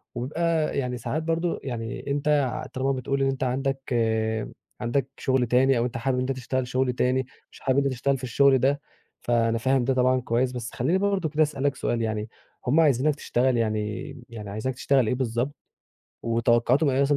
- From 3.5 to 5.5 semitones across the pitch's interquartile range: No, narrow, 2.5 semitones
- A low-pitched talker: Yes, low, 130 Hz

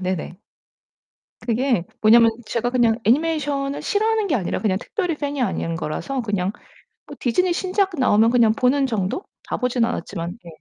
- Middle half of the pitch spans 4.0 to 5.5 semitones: Yes, average, 5.1 semitones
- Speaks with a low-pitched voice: No, high, 245 Hz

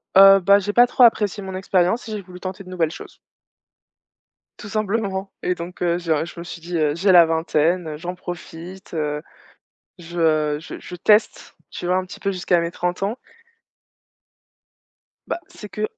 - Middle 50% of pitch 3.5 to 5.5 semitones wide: No, average, 2.7 semitones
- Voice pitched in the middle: Yes, medium, 180 Hz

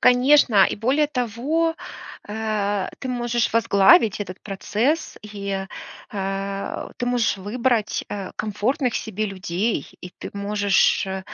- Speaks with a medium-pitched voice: No, high, 215 Hz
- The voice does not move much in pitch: No, average, 3.7 semitones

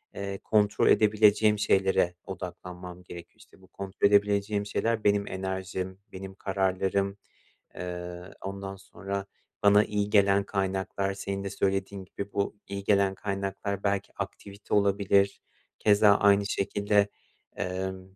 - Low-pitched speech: Yes, low, 100 Hz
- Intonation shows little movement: Yes, narrow, 1.1 semitones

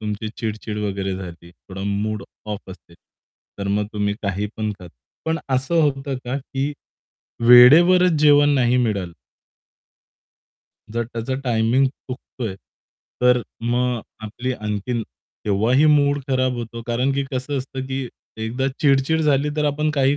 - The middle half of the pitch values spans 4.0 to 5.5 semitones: Yes, average, 4.3 semitones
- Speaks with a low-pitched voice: Yes, low, 125 Hz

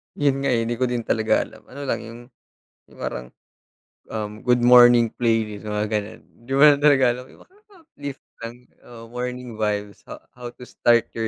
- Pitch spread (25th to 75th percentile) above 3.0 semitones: No, narrow, 2.4 semitones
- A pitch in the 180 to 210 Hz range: No, low, 120 Hz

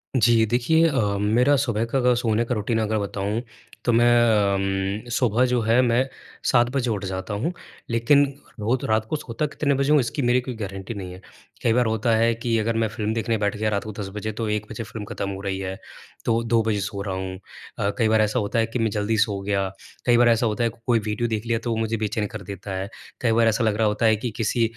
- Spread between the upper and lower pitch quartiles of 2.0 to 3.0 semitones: Yes, narrow, 2.4 semitones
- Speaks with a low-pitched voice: Yes, low, 110 Hz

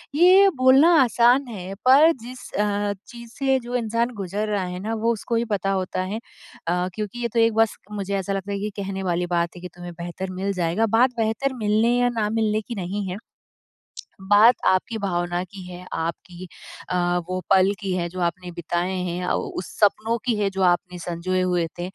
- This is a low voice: No, high, 200 Hz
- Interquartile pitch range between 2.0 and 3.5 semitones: No, average, 4.1 semitones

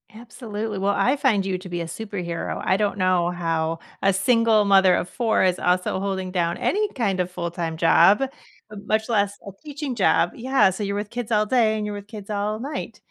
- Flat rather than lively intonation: No, average, 3.4 semitones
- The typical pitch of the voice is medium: No, high, 200 Hz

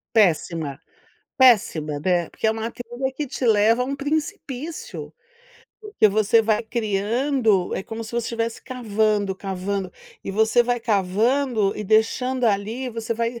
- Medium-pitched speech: No, high, 225 Hz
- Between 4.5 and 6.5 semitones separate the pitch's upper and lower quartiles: No, average, 3.6 semitones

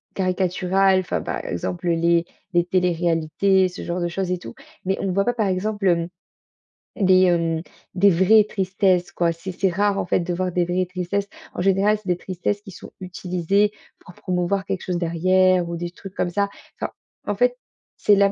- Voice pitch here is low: No, medium, 185 Hz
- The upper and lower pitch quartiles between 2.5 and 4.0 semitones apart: No, narrow, 2.0 semitones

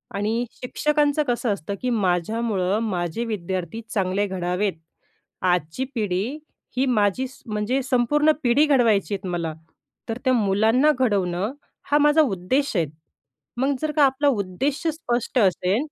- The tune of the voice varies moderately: No, wide, 5.7 semitones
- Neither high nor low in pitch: No, high, 225 Hz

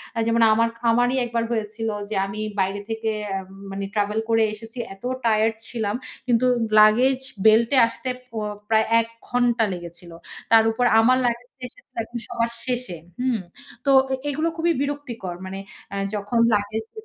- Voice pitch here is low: No, high, 225 Hz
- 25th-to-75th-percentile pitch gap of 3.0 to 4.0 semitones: No, narrow, 2.5 semitones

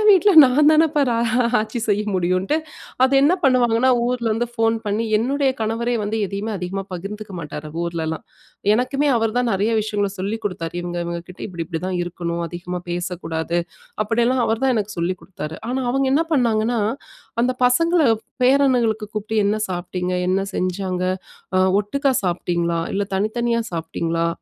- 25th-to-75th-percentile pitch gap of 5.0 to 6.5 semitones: Yes, wide, 5.4 semitones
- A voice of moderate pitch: No, high, 210 Hz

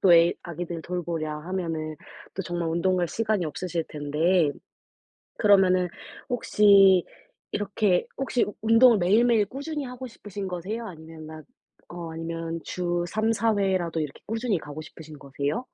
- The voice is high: No, medium, 180 Hz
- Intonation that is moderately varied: Yes, average, 4.3 semitones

